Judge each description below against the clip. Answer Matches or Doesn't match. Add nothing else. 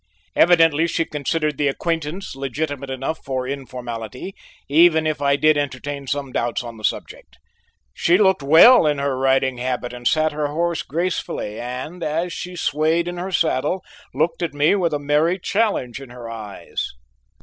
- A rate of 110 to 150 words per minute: Doesn't match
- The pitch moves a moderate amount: Matches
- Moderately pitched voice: Matches